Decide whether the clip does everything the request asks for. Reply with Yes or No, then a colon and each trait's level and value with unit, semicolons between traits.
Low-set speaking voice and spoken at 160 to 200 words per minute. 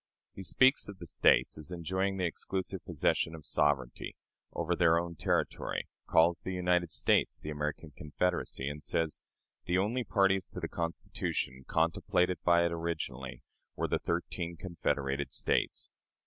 No: very low, 85 Hz; average, 150 wpm